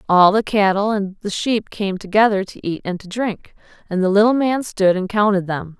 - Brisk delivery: Yes, fast, 215 wpm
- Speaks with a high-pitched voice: Yes, high, 200 Hz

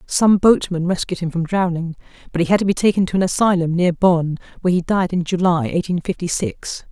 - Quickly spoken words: Yes, fast, 215 wpm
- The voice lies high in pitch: No, medium, 175 Hz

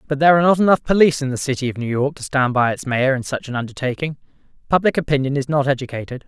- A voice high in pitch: No, medium, 140 Hz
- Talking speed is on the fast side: Yes, fast, 250 wpm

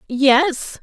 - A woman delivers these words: Yes, female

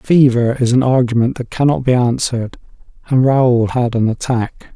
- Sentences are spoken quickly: No, average, 165 wpm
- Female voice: No, male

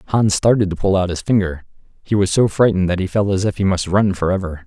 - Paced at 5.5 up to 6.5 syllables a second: Yes, 6.1 syllables/s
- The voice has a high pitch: No, very low, 95 Hz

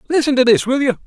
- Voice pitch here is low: No, very high, 250 Hz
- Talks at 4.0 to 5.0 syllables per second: No, 7.1 syllables/s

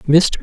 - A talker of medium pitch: Yes, medium, 160 Hz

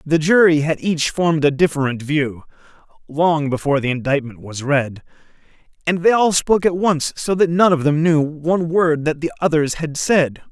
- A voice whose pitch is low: No, medium, 155 Hz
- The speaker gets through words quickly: No, average, 190 wpm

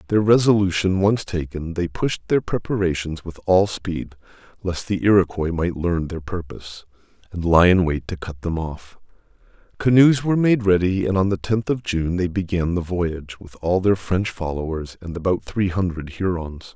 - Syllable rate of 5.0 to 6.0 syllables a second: No, 4.8 syllables/s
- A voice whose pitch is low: Yes, very low, 90 Hz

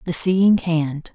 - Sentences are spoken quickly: No, average, 155 wpm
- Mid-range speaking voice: Yes, medium, 170 Hz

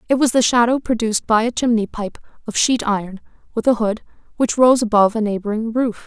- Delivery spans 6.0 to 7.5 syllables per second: Yes, 6.1 syllables/s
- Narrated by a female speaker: Yes, female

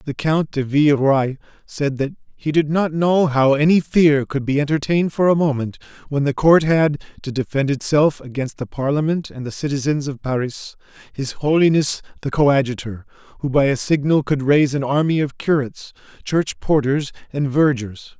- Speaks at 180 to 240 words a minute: No, average, 170 wpm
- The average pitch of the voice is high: No, medium, 145 Hz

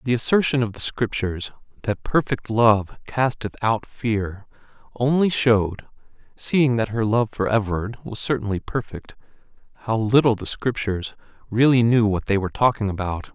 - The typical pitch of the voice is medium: No, low, 110 Hz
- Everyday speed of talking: Yes, average, 150 wpm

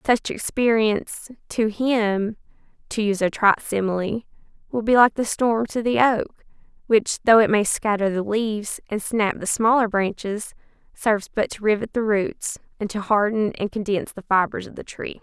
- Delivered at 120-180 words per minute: Yes, average, 175 wpm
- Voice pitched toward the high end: Yes, high, 215 Hz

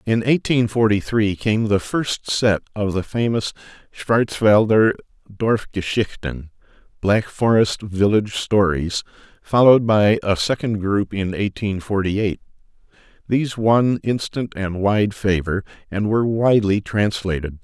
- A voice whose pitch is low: Yes, low, 105 Hz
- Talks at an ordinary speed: No, slow, 120 wpm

